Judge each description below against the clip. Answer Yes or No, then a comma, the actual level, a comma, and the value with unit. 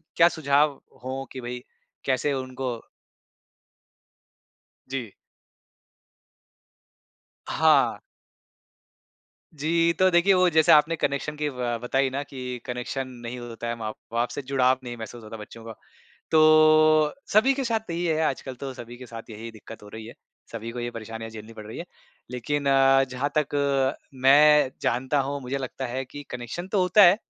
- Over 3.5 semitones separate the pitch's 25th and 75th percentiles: Yes, average, 3.9 semitones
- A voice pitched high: No, low, 135 Hz